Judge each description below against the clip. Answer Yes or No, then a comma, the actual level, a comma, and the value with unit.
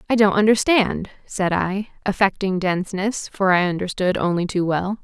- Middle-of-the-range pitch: No, high, 195 Hz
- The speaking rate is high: No, average, 155 wpm